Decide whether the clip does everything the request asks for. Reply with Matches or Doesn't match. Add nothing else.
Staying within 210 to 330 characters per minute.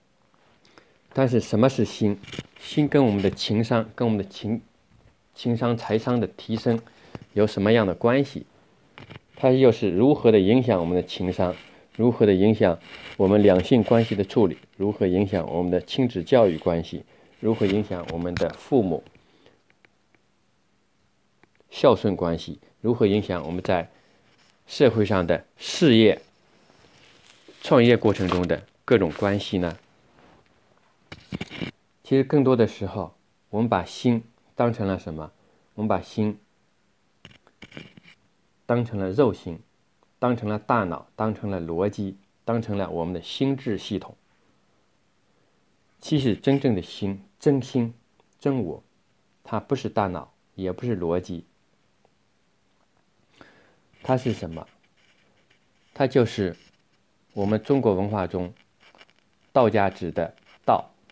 Doesn't match